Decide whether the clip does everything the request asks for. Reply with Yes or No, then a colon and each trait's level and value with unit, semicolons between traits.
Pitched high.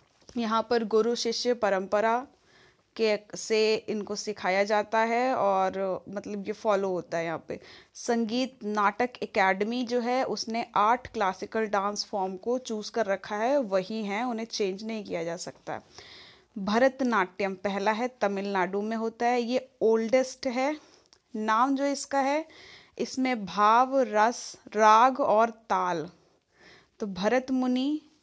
Yes: high, 220 Hz